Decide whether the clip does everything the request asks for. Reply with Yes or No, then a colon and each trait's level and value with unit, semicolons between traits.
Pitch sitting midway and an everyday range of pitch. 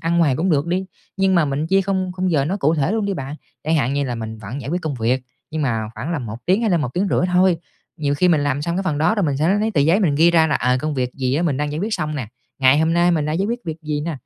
Yes: medium, 155 Hz; average, 4.2 semitones